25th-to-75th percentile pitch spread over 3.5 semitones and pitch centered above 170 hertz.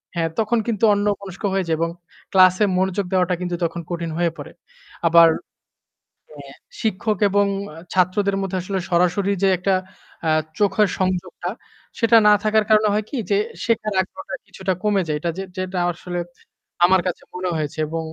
No: average, 2.7 semitones; medium, 185 Hz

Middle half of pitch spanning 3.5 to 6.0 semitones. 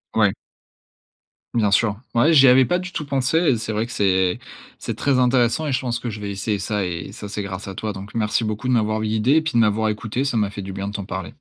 Yes: average, 3.9 semitones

